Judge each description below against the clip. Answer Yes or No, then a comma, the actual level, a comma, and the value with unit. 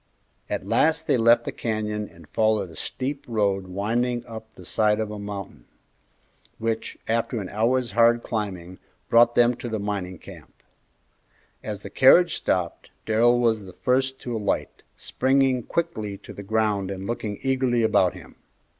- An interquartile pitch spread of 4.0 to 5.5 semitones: No, average, 3.0 semitones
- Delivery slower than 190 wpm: Yes, average, 160 wpm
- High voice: No, low, 110 Hz